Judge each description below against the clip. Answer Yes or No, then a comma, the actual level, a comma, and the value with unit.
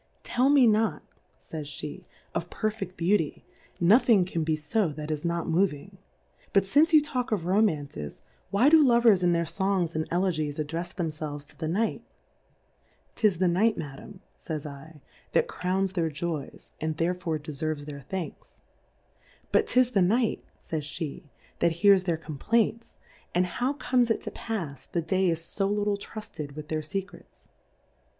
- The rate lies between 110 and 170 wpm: Yes, average, 160 wpm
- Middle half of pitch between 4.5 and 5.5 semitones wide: Yes, average, 5.0 semitones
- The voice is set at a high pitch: No, medium, 175 Hz